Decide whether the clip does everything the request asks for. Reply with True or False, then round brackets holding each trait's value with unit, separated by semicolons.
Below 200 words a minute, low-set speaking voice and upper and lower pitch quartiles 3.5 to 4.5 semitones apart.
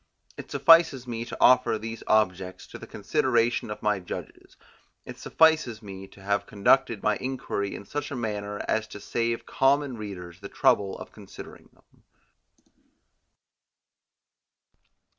True (140 wpm; 110 Hz; 4.0 semitones)